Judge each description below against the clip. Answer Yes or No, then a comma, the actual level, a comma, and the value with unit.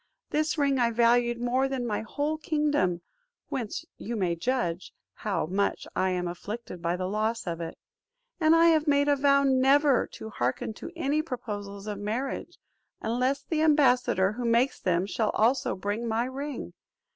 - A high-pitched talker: Yes, high, 240 Hz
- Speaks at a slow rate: No, average, 170 wpm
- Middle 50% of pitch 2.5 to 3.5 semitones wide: No, wide, 5.5 semitones